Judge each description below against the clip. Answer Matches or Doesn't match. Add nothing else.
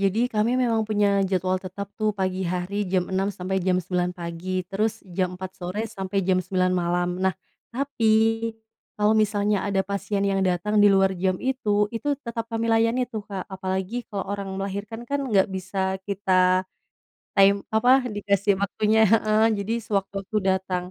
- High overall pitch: Matches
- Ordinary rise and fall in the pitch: Doesn't match